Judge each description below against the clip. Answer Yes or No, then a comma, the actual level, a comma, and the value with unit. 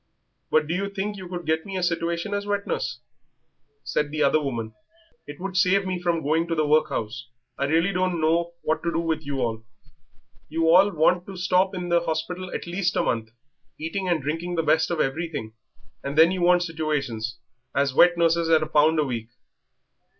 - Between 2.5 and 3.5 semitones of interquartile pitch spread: Yes, average, 3.1 semitones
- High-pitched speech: No, medium, 165 Hz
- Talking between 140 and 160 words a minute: No, average, 200 wpm